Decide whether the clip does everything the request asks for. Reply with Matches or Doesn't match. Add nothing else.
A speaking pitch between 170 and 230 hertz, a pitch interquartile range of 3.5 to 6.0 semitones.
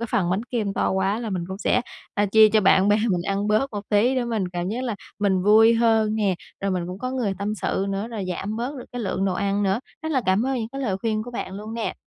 Doesn't match